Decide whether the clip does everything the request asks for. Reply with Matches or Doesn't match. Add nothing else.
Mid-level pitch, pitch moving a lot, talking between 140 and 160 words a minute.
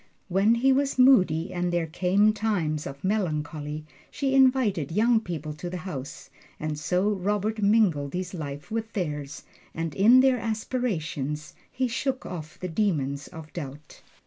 Matches